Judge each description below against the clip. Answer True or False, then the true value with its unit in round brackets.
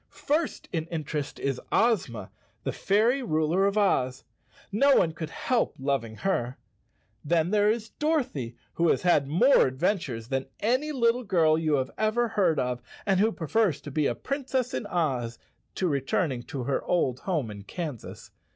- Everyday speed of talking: True (165 wpm)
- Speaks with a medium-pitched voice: True (170 Hz)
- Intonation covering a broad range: True (8.2 semitones)